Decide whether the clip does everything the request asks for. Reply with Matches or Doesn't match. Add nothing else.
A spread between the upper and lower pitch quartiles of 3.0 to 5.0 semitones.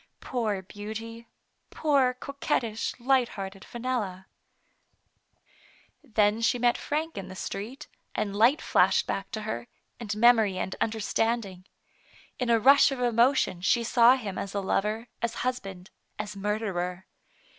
Matches